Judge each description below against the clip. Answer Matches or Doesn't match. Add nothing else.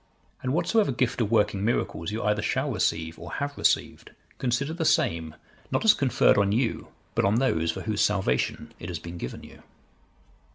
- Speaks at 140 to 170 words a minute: Doesn't match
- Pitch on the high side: Doesn't match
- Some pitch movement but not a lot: Doesn't match